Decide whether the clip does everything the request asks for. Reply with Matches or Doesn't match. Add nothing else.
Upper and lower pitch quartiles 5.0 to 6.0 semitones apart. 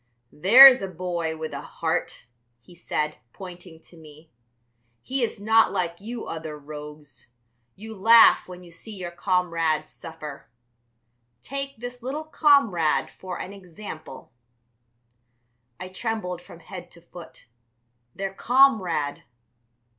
Matches